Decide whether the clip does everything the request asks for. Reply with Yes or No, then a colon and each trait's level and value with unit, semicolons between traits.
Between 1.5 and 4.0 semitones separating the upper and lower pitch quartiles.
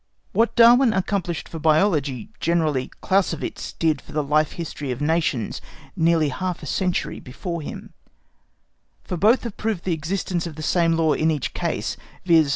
Yes: average, 3.5 semitones